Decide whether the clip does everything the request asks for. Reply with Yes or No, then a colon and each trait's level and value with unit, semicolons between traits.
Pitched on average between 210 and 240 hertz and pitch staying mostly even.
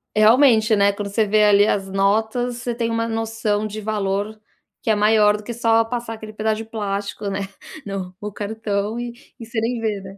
Yes: high, 215 Hz; narrow, 1.9 semitones